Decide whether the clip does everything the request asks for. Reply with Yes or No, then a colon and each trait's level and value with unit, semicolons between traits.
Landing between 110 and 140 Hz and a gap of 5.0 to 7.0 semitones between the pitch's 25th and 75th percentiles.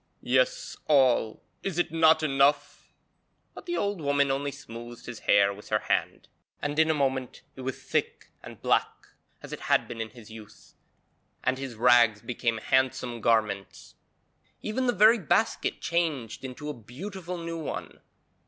Yes: low, 135 Hz; wide, 5.5 semitones